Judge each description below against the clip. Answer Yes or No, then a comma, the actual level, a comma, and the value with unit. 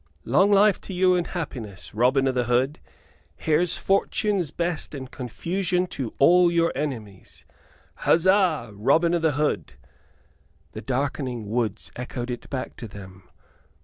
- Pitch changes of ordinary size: No, wide, 6.4 semitones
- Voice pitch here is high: No, medium, 140 Hz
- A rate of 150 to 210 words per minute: No, average, 140 wpm